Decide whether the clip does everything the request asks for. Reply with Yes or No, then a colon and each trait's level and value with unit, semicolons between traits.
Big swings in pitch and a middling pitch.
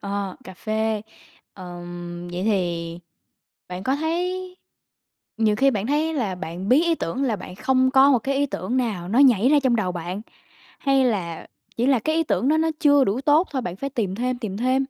No: wide, 6.6 semitones; high, 230 Hz